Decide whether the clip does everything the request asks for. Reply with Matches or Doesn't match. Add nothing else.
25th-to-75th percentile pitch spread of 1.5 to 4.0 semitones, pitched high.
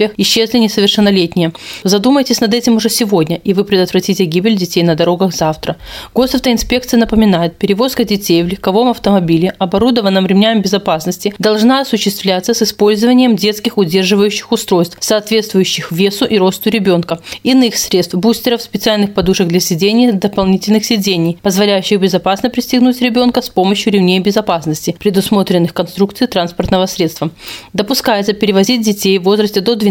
Matches